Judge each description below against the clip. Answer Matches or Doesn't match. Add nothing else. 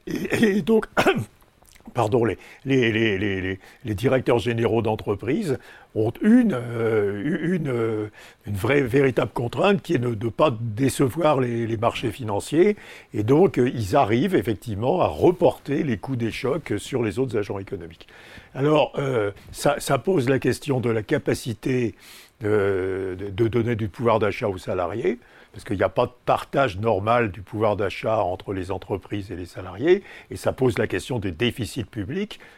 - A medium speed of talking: Matches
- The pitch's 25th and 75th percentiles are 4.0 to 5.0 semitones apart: Matches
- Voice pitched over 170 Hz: Doesn't match